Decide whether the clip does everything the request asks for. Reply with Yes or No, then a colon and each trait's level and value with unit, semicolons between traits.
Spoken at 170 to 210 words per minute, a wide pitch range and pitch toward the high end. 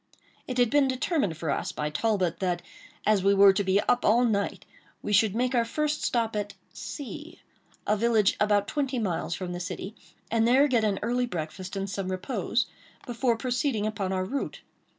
No: average, 190 wpm; average, 4.3 semitones; high, 215 Hz